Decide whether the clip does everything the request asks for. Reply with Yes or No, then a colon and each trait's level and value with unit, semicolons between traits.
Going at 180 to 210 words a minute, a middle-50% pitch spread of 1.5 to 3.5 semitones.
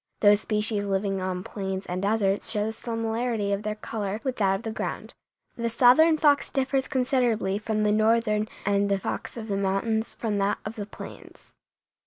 Yes: average, 185 wpm; narrow, 2.5 semitones